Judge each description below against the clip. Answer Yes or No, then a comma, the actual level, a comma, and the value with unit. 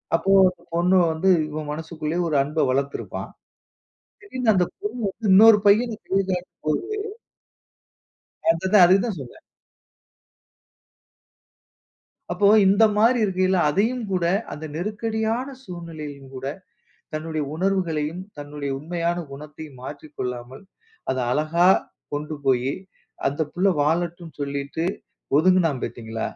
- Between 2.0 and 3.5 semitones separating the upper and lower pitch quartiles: No, average, 4.5 semitones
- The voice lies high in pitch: No, medium, 165 Hz